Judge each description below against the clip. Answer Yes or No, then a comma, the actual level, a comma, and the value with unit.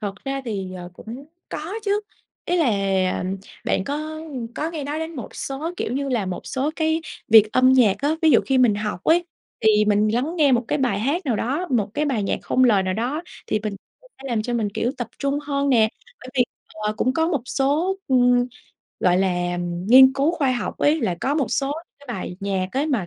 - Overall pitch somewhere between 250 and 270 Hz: Yes, very high, 255 Hz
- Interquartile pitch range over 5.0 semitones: Yes, wide, 5.4 semitones